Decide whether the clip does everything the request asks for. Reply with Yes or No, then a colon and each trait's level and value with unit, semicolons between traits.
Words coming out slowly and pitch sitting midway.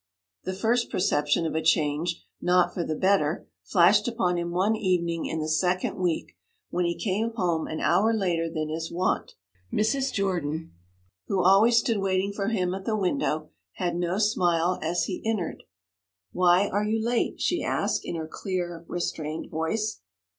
No: average, 170 wpm; medium, 180 Hz